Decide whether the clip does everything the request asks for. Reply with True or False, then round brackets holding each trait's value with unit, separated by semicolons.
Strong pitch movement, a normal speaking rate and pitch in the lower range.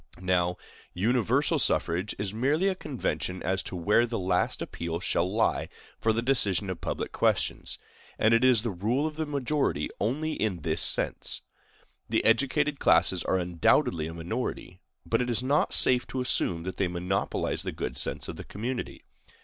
True (6.1 semitones; 175 wpm; 110 Hz)